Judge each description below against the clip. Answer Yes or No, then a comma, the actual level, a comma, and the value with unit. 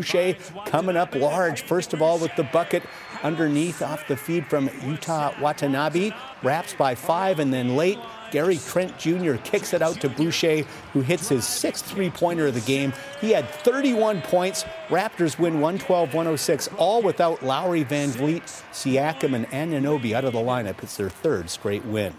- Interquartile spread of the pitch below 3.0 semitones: No, average, 4.1 semitones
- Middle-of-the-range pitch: Yes, medium, 160 Hz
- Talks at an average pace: Yes, average, 170 wpm